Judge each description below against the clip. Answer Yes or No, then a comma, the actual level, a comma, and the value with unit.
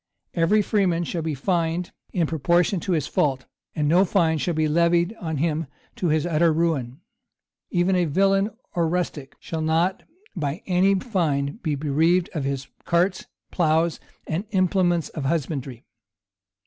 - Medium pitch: Yes, medium, 165 Hz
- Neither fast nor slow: Yes, average, 150 wpm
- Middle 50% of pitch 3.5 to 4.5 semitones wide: No, average, 2.8 semitones